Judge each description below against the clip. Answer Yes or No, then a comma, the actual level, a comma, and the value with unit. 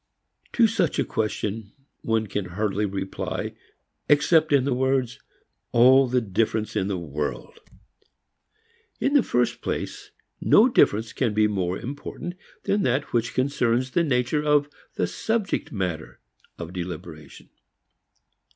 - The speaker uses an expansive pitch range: Yes, wide, 6.4 semitones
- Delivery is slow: Yes, slow, 130 wpm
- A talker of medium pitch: No, low, 120 Hz